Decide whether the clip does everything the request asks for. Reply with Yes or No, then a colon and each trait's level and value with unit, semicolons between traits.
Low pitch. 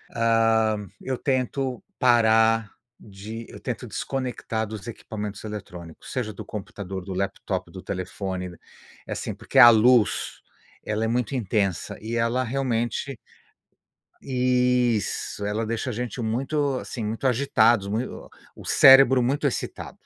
Yes: low, 115 Hz